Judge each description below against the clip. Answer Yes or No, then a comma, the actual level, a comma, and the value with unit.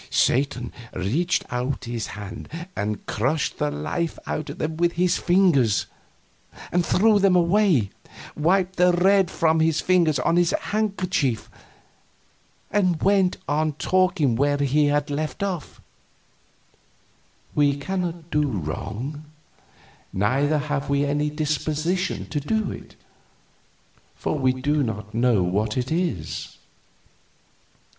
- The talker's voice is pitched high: No, medium, 150 Hz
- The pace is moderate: No, slow, 120 wpm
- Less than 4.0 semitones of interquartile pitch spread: No, wide, 5.6 semitones